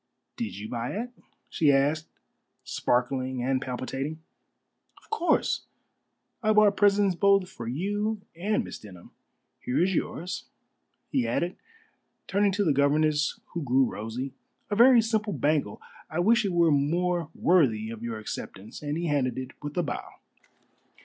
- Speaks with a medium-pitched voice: Yes, medium, 155 Hz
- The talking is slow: No, average, 150 wpm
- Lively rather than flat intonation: Yes, wide, 7.3 semitones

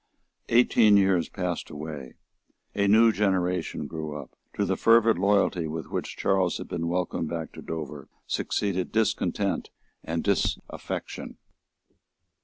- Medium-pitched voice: No, very low, 90 Hz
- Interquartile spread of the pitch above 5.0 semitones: No, average, 3.9 semitones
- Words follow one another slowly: Yes, slow, 125 wpm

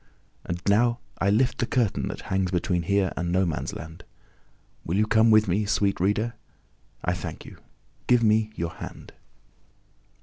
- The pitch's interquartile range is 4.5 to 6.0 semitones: No, average, 3.6 semitones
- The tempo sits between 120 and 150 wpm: No, average, 165 wpm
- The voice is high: No, low, 100 Hz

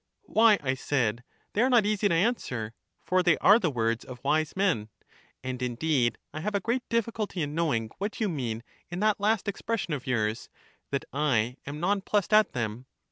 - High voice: No, medium, 155 Hz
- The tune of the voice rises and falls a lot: Yes, wide, 8.8 semitones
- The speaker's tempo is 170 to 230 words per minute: Yes, average, 200 wpm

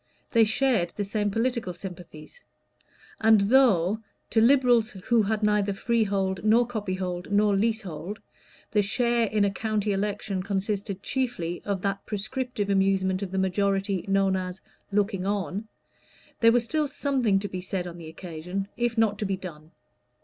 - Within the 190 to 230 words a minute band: No, average, 155 wpm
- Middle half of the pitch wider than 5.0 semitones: No, average, 2.8 semitones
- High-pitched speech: Yes, high, 200 Hz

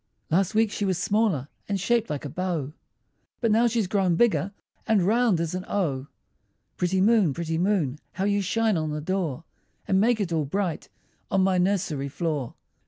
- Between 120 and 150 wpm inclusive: No, average, 180 wpm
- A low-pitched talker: No, medium, 185 Hz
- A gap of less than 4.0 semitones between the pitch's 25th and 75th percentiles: No, average, 4.3 semitones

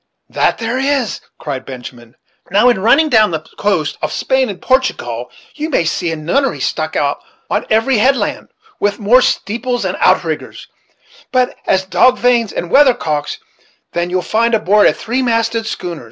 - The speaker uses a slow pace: No, average, 170 wpm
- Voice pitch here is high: Yes, high, 220 Hz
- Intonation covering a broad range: Yes, wide, 6.6 semitones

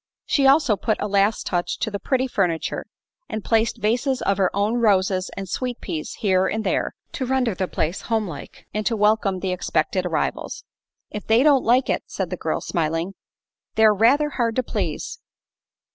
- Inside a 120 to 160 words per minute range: No, average, 180 wpm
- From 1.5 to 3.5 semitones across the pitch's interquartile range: No, average, 4.3 semitones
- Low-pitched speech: No, high, 210 Hz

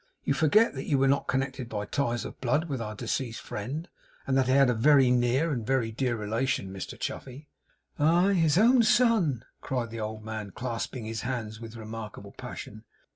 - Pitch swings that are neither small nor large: Yes, average, 4.1 semitones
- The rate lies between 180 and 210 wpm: Yes, average, 190 wpm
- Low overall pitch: Yes, low, 125 Hz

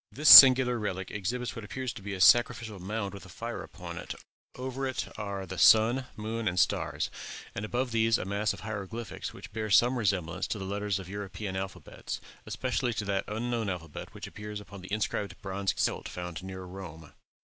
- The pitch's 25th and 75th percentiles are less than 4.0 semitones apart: Yes, average, 3.2 semitones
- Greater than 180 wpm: Yes, average, 195 wpm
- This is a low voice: Yes, low, 105 Hz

